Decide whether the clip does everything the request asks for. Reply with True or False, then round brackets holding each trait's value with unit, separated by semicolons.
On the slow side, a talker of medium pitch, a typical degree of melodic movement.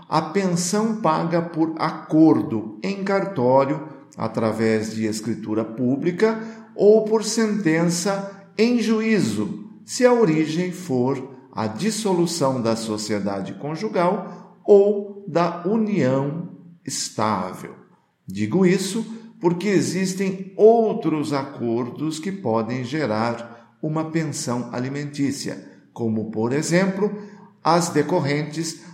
False (95 wpm; 160 Hz; 7.2 semitones)